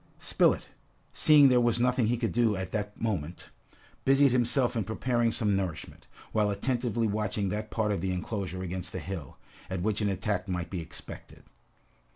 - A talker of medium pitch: No, low, 105 Hz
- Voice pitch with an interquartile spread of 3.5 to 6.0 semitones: Yes, average, 4.1 semitones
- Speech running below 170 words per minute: No, average, 175 wpm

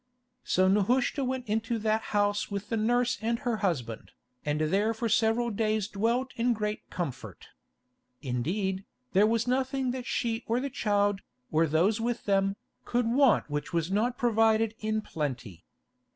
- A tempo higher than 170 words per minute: No, average, 155 wpm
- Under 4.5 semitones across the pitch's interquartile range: Yes, average, 3.5 semitones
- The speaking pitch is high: Yes, high, 215 Hz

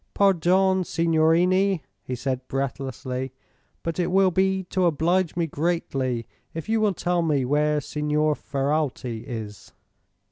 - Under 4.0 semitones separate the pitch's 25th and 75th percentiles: No, average, 5.0 semitones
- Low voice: No, medium, 160 Hz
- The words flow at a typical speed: No, slow, 130 wpm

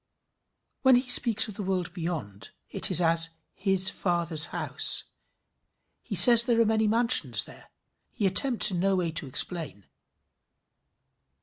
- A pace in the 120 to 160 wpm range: Yes, average, 140 wpm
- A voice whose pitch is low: No, medium, 185 Hz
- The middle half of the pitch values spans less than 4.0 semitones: No, average, 5.0 semitones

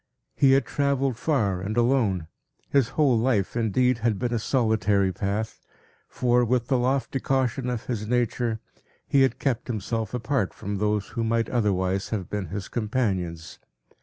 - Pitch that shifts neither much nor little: Yes, average, 3.7 semitones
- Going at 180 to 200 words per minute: No, average, 160 wpm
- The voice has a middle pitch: No, low, 115 Hz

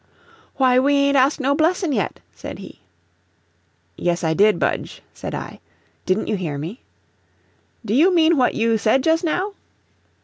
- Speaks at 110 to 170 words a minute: Yes, average, 160 wpm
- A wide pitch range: Yes, wide, 6.9 semitones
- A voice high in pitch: Yes, very high, 260 Hz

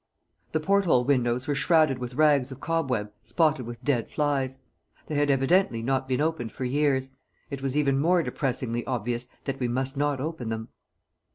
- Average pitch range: Yes, average, 3.1 semitones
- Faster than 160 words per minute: Yes, average, 180 wpm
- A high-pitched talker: No, low, 135 Hz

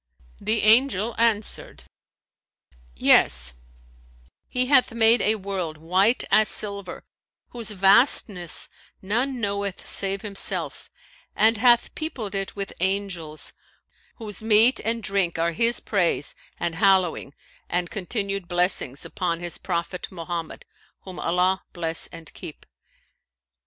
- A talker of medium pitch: No, high, 195 Hz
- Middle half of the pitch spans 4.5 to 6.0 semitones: No, average, 4.0 semitones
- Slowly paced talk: Yes, slow, 115 wpm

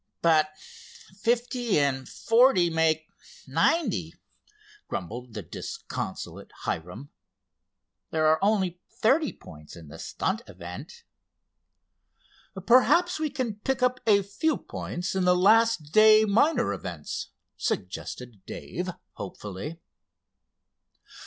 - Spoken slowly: Yes, slow, 100 wpm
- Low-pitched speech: No, medium, 180 Hz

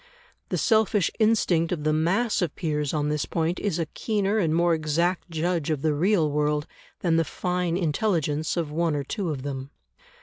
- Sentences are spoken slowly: No, average, 190 wpm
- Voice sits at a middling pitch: Yes, medium, 165 Hz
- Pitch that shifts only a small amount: No, average, 3.2 semitones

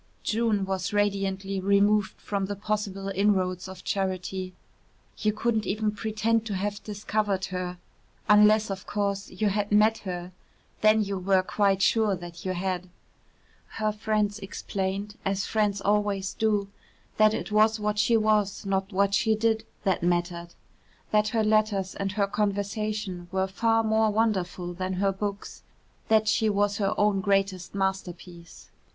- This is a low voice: No, high, 200 Hz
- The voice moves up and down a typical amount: No, narrow, 1.9 semitones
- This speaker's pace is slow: No, average, 150 wpm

